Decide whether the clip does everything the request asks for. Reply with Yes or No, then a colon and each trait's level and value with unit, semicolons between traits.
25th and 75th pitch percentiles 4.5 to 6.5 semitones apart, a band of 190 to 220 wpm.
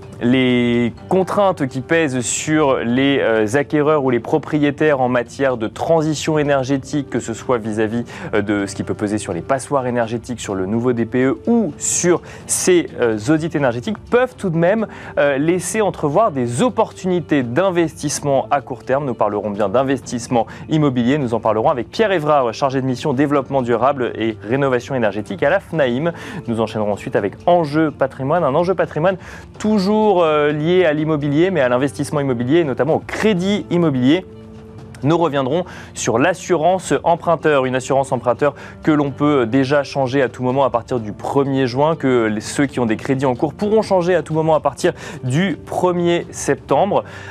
No: average, 4.9 semitones; average, 170 wpm